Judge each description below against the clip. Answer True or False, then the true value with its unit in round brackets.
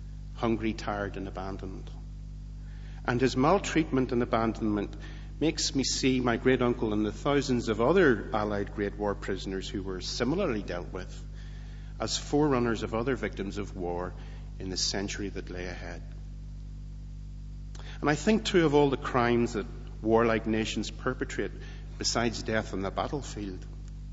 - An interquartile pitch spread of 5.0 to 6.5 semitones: True (5.4 semitones)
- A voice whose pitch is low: True (105 Hz)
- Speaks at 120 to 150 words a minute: True (145 wpm)